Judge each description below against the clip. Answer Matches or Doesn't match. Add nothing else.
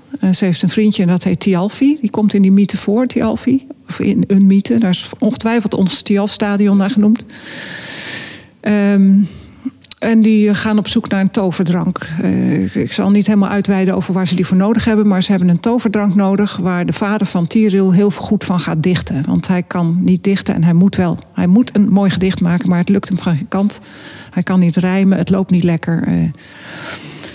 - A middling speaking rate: Doesn't match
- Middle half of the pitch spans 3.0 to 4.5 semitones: Doesn't match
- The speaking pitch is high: Matches